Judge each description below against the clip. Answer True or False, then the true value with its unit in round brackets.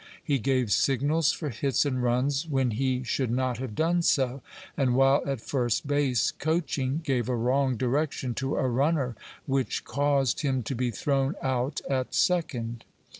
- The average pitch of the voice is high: False (135 Hz)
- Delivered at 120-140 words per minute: False (165 wpm)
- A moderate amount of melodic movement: False (2.2 semitones)